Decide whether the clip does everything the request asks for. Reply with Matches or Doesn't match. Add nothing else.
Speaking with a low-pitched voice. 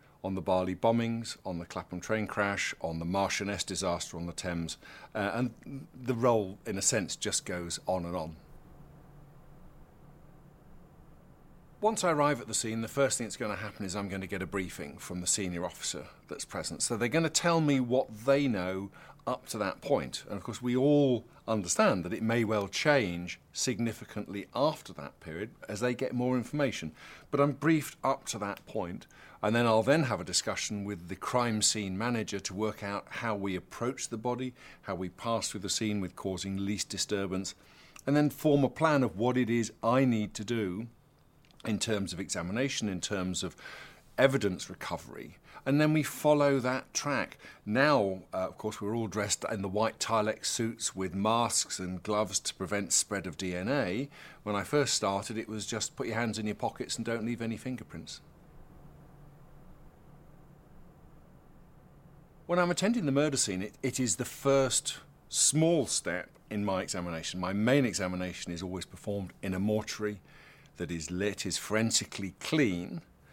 Matches